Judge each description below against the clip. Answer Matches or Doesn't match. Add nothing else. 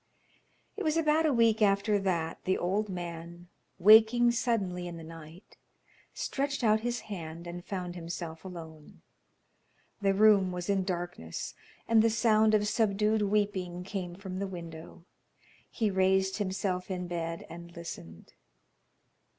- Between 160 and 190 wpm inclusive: Doesn't match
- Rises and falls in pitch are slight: Doesn't match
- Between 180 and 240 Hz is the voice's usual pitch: Matches